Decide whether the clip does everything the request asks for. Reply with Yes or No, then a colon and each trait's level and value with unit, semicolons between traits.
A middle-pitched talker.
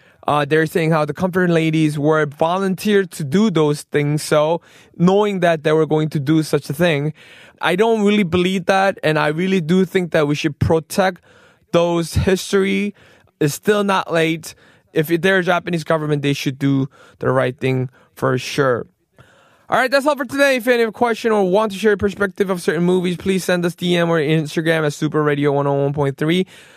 Yes: medium, 170 Hz